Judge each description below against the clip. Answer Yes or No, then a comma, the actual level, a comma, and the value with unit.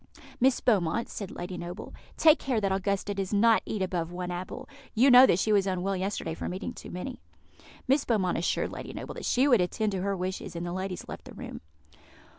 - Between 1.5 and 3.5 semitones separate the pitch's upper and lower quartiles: No, average, 4.1 semitones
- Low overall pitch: No, high, 195 Hz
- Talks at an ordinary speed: No, fast, 215 wpm